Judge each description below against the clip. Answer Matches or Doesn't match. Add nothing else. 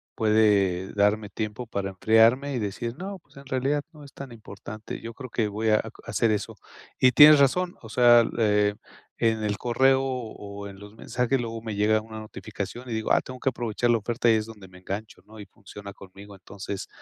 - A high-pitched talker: Doesn't match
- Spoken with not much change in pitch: Doesn't match